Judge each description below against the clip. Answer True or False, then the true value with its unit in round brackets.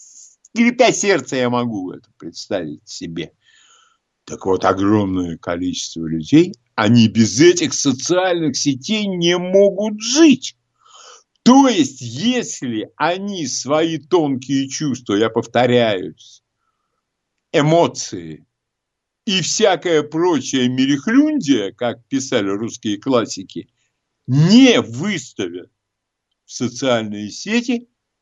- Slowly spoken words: True (90 wpm)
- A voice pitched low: False (160 Hz)